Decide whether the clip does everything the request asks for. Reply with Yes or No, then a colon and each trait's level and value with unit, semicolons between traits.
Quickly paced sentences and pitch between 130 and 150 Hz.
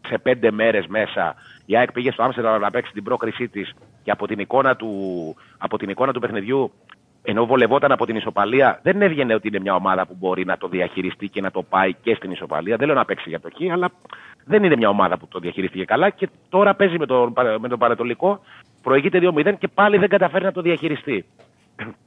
No: fast, 205 wpm; low, 120 Hz